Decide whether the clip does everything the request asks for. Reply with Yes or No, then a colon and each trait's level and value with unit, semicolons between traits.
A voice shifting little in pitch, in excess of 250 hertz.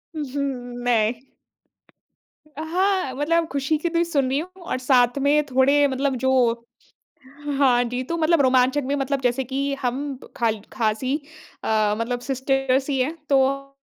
Yes: narrow, 2.3 semitones; very high, 270 Hz